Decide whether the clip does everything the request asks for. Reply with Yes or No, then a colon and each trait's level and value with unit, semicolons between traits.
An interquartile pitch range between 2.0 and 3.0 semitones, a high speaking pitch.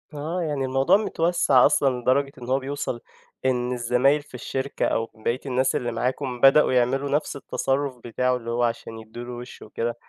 No: narrow, 2.4 semitones; low, 130 Hz